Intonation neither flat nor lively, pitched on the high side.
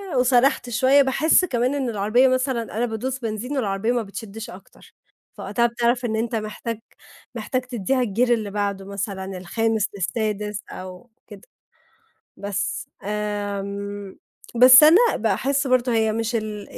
Yes: average, 3.5 semitones; high, 225 Hz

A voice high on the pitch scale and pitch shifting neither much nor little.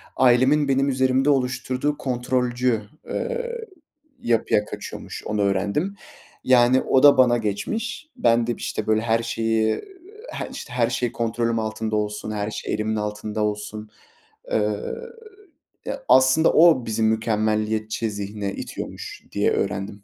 No: low, 115 Hz; average, 3.2 semitones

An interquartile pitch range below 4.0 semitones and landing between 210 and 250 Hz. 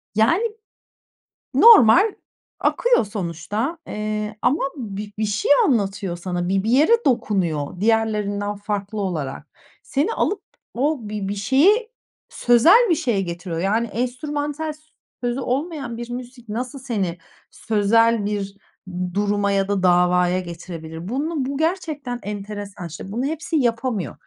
No: wide, 5.4 semitones; high, 220 Hz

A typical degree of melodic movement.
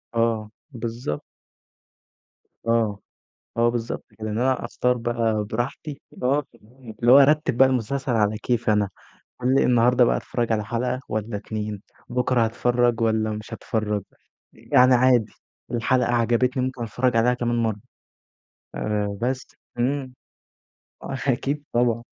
No: narrow, 2.3 semitones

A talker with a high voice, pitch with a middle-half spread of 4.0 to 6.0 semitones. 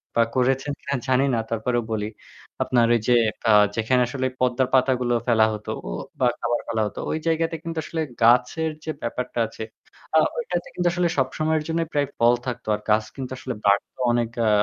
No: low, 125 Hz; average, 4.8 semitones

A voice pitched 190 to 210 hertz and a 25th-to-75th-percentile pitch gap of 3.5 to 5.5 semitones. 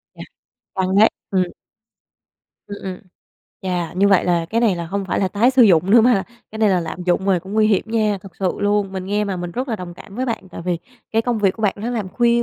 No: high, 200 Hz; average, 3.1 semitones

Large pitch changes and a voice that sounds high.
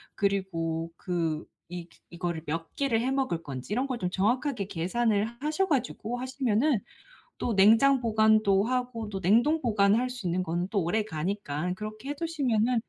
Yes: wide, 5.8 semitones; high, 215 Hz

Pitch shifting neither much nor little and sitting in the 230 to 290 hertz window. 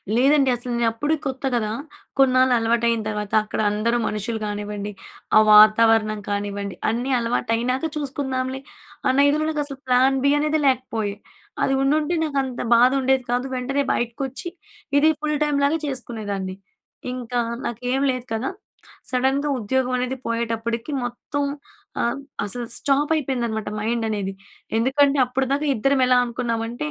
Yes: average, 3.2 semitones; very high, 250 Hz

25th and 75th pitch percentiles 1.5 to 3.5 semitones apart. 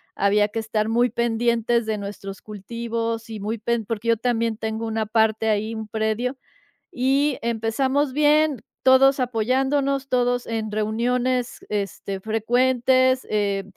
Yes: narrow, 2.5 semitones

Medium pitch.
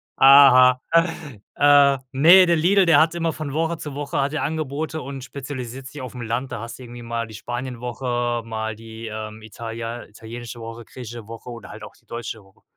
No: low, 125 Hz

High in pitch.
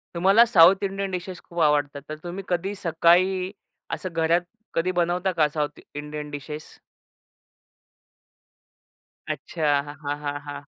No: medium, 165 Hz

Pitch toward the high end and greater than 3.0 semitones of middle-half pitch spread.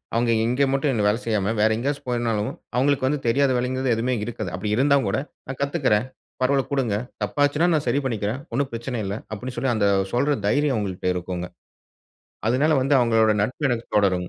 No: low, 120 Hz; average, 4.4 semitones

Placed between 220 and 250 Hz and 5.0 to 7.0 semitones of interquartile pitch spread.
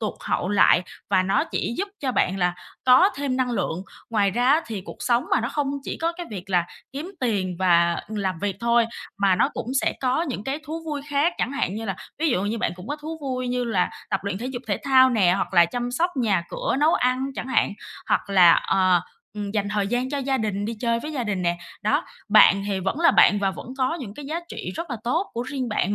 Yes: high, 235 Hz; wide, 5.4 semitones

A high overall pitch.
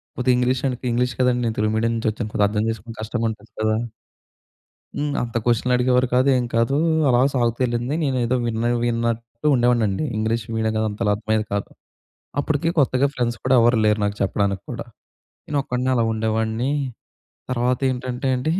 No: low, 120 Hz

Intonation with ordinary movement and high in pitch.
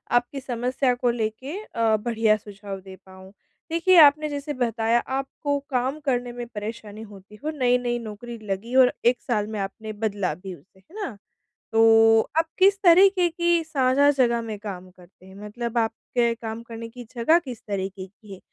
Yes: average, 4.1 semitones; high, 235 Hz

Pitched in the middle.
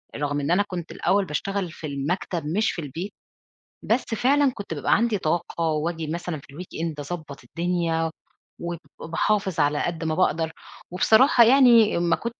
Yes: medium, 170 Hz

